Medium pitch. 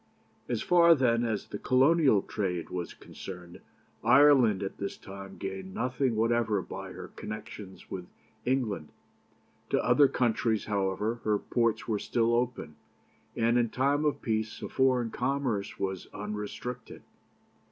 No: low, 110 Hz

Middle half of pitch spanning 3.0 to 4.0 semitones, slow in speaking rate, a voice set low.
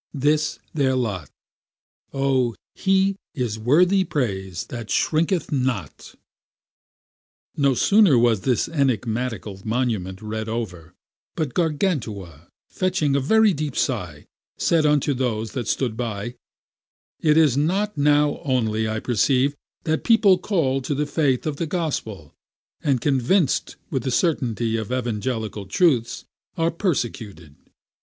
No: wide, 5.6 semitones; slow, 125 wpm; low, 130 Hz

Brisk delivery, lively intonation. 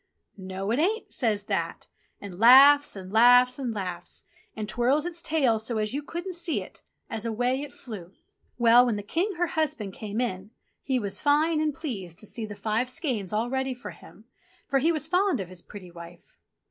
Yes: fast, 210 wpm; wide, 5.8 semitones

